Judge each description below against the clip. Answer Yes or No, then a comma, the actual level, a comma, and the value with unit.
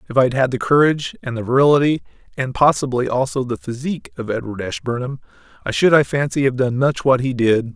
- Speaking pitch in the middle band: No, low, 130 Hz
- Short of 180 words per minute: No, average, 200 wpm